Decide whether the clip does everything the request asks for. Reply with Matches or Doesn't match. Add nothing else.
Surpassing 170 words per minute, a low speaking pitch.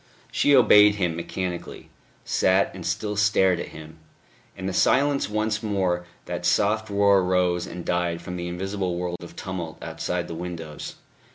Doesn't match